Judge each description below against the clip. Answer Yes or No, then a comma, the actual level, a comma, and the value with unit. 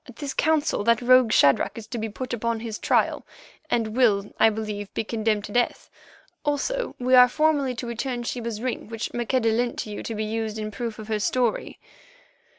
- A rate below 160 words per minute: No, average, 200 wpm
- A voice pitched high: Yes, high, 230 Hz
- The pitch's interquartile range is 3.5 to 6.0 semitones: No, average, 2.7 semitones